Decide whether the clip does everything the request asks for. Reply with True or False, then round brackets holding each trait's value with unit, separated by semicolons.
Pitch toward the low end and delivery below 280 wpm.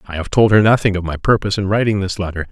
False (100 Hz; 285 wpm)